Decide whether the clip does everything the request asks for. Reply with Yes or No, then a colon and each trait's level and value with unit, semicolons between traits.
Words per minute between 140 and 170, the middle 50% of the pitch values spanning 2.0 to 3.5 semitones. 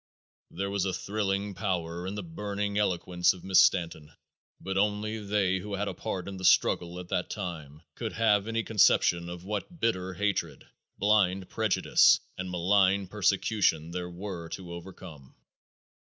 Yes: average, 155 wpm; average, 2.7 semitones